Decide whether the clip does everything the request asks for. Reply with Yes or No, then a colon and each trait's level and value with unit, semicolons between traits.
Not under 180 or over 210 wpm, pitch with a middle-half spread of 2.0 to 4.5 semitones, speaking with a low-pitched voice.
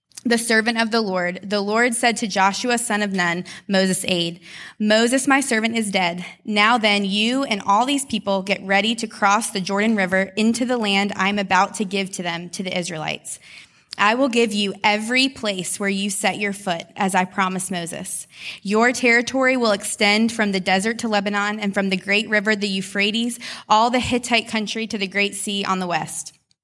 No: average, 200 wpm; average, 2.8 semitones; high, 205 Hz